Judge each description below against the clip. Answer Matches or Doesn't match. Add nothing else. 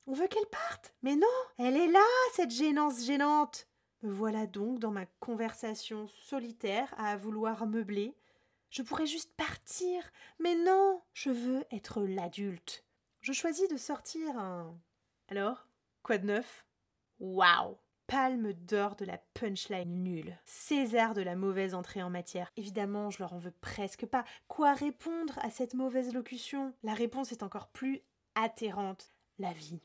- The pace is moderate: Matches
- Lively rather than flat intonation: Matches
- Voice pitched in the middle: Doesn't match